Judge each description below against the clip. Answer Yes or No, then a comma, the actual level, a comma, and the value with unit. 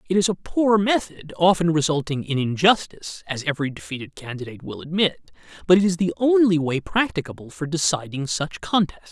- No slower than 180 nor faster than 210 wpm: No, average, 170 wpm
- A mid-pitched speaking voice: Yes, medium, 165 Hz